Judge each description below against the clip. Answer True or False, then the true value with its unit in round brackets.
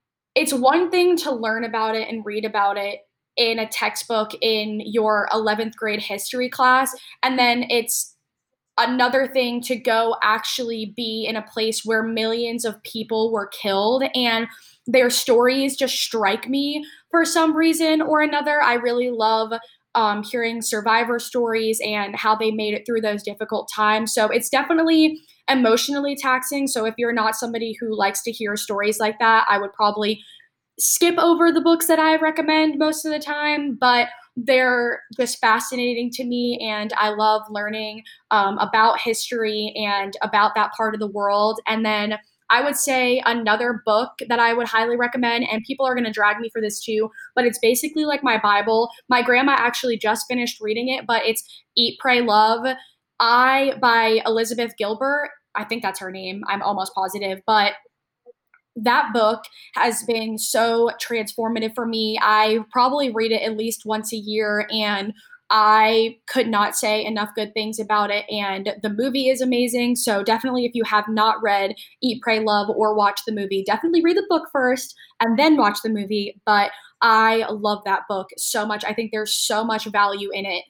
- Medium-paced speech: True (180 wpm)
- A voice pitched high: True (225 Hz)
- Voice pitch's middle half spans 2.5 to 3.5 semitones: True (2.8 semitones)